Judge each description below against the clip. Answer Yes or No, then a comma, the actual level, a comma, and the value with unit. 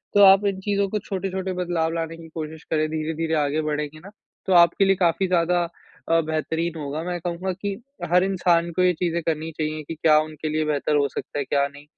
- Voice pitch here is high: No, medium, 165 Hz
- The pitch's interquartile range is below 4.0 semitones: Yes, average, 2.7 semitones